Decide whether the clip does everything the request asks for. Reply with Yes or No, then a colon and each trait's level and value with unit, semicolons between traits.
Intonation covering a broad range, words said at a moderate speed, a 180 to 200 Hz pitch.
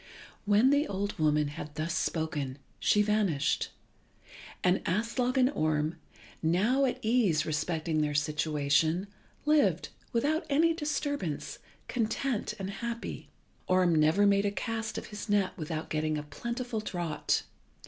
No: wide, 7.0 semitones; slow, 130 wpm; high, 190 Hz